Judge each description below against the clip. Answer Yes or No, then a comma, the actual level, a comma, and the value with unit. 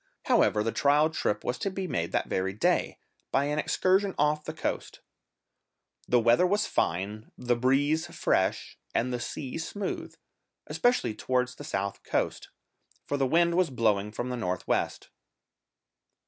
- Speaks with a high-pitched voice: No, low, 130 Hz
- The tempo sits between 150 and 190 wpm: Yes, average, 155 wpm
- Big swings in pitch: Yes, wide, 6.7 semitones